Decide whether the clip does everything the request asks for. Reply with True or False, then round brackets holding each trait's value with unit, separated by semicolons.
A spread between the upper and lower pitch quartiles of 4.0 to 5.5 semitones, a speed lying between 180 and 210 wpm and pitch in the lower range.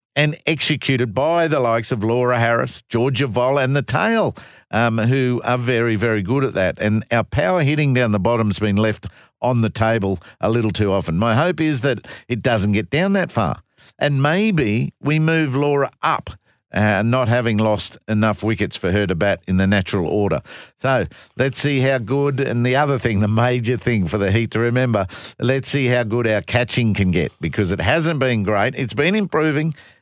True (4.4 semitones; 200 wpm; 120 Hz)